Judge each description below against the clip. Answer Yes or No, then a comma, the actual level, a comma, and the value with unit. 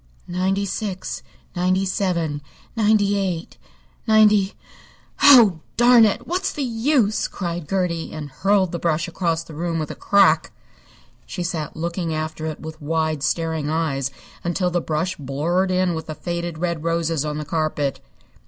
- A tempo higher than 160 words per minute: No, average, 155 wpm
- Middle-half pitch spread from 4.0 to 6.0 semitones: No, average, 3.5 semitones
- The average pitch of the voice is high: No, medium, 170 Hz